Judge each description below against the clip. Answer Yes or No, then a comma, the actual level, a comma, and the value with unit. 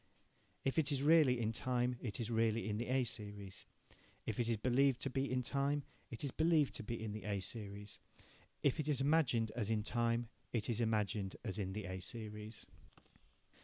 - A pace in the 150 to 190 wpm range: No, average, 200 wpm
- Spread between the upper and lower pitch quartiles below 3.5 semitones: No, average, 3.9 semitones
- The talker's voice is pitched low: Yes, low, 115 Hz